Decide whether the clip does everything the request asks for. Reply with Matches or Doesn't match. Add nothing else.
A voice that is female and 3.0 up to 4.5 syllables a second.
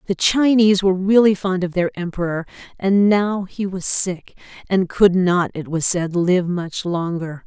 Matches